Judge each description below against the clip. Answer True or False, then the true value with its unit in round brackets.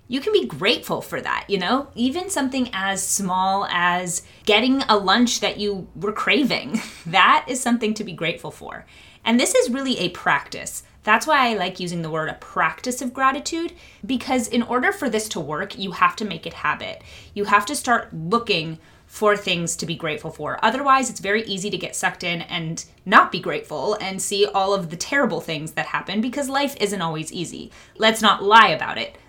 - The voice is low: False (205 Hz)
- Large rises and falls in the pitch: True (5.7 semitones)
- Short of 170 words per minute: False (205 wpm)